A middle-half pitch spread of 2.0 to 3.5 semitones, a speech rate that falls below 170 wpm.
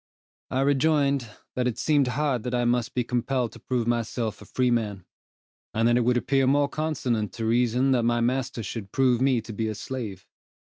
No: narrow, 2.4 semitones; average, 195 wpm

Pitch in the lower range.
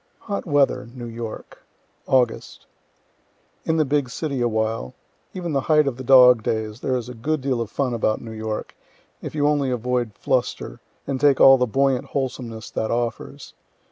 Yes: low, 125 Hz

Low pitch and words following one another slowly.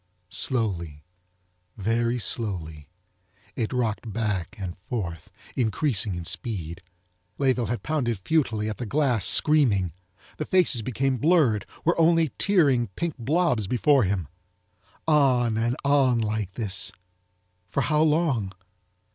Yes: low, 115 Hz; slow, 115 wpm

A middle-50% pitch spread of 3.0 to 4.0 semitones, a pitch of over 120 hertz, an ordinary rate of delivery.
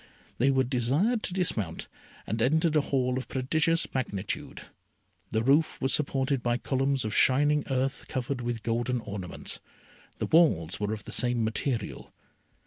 Yes: average, 3.6 semitones; low, 130 Hz; average, 150 wpm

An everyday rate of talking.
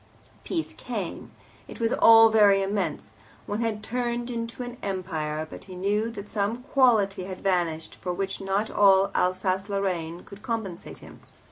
Yes: average, 155 wpm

